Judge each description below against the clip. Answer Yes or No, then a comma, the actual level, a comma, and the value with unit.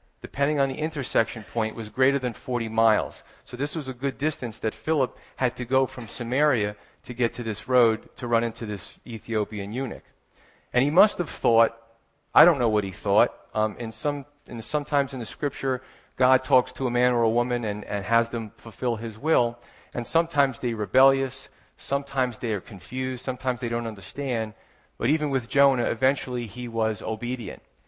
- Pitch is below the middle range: Yes, low, 120 Hz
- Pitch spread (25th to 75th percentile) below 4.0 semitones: Yes, average, 2.8 semitones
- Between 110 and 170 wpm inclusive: No, average, 190 wpm